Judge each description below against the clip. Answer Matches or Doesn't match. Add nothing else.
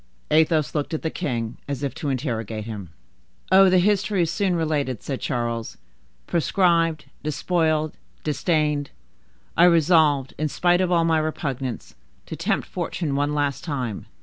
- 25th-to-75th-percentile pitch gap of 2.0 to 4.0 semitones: Matches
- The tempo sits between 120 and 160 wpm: Matches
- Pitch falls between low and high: Matches